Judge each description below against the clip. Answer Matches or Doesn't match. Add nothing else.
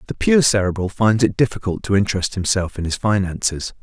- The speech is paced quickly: Doesn't match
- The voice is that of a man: Matches